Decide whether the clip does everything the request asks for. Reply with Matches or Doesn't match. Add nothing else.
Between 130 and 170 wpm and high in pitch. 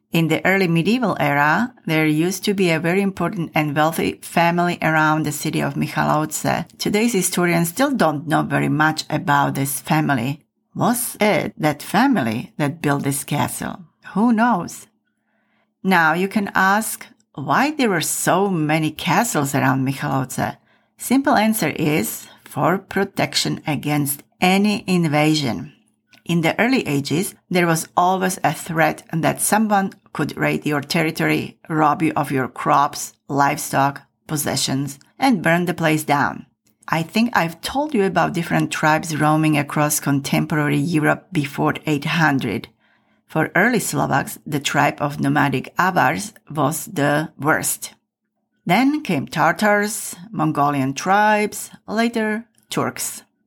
Doesn't match